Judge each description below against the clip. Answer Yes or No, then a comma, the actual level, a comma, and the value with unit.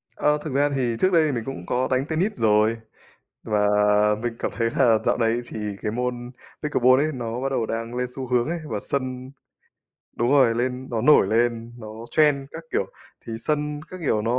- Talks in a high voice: No, low, 125 Hz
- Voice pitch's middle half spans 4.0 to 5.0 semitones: No, average, 3.5 semitones